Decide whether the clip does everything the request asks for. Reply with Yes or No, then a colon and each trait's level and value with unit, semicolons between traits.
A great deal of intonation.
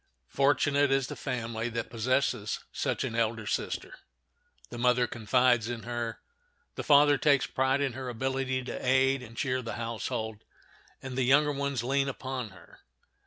No: average, 2.7 semitones